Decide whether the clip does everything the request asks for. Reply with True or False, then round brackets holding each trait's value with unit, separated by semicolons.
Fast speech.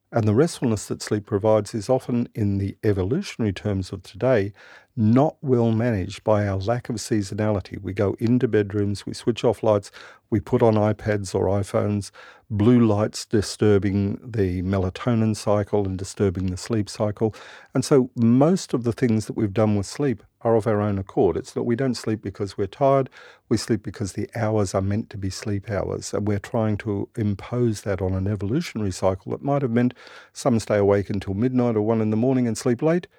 False (195 wpm)